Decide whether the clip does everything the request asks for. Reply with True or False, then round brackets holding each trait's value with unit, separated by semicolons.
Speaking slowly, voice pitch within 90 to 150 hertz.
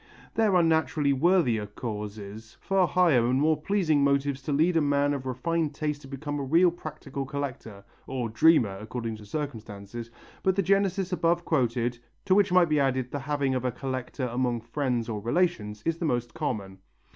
False (180 wpm; 140 Hz)